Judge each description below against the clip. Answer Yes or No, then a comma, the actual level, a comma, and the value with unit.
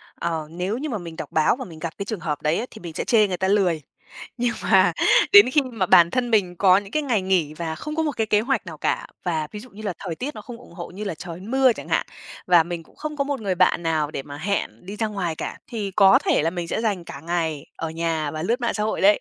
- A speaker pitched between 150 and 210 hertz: Yes, medium, 185 Hz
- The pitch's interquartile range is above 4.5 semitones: Yes, average, 5.0 semitones